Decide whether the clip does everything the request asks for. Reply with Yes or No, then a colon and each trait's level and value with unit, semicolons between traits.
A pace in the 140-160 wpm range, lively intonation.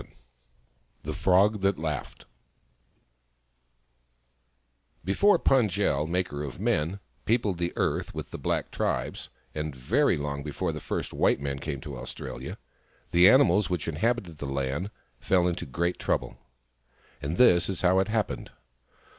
No: average, 145 wpm; average, 4.9 semitones